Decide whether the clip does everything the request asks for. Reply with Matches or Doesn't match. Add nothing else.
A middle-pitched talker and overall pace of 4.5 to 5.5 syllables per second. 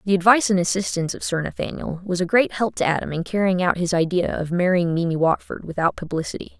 Doesn't match